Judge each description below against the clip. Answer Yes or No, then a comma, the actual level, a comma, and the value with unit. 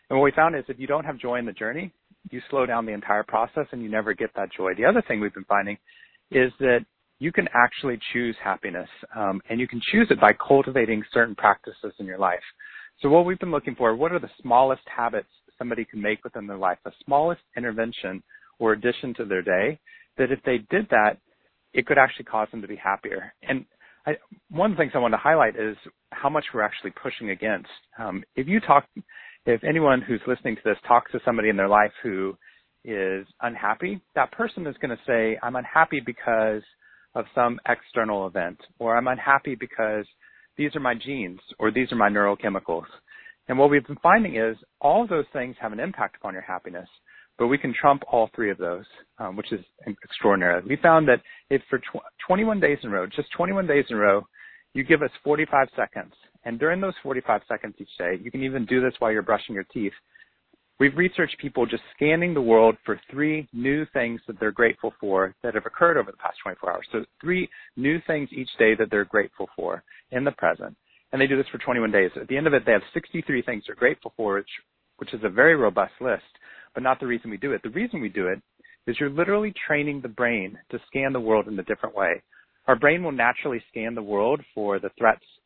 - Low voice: Yes, low, 125 Hz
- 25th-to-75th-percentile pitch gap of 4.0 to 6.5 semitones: Yes, average, 4.9 semitones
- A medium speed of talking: No, fast, 225 wpm